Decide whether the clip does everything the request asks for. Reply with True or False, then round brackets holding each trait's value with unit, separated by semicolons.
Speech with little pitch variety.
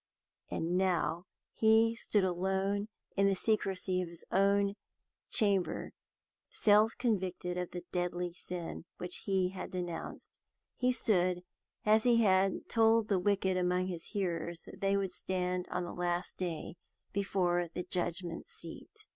True (2.1 semitones)